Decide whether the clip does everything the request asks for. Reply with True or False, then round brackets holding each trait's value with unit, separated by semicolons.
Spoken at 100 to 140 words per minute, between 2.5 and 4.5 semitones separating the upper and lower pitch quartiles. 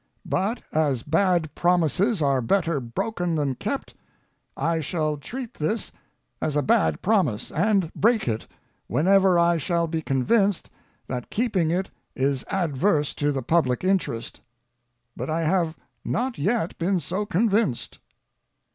False (135 wpm; 5.0 semitones)